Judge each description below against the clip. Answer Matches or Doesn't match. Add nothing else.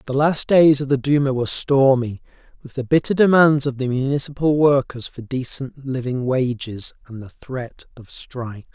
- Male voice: Matches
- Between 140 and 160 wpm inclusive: Doesn't match